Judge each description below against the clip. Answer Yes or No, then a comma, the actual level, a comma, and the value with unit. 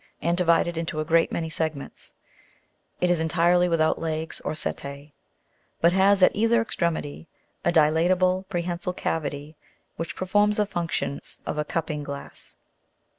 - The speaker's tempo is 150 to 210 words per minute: No, average, 140 wpm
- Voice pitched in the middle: Yes, medium, 165 Hz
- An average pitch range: No, narrow, 2.3 semitones